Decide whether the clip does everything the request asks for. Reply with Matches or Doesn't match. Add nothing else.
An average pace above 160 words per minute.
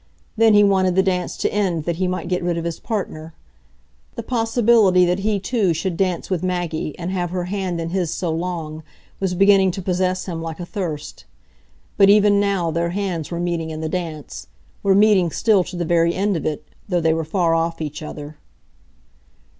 Matches